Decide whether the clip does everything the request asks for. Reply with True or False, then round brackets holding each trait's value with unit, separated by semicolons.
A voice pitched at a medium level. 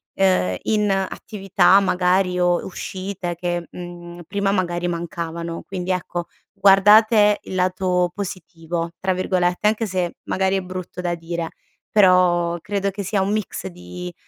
True (180 Hz)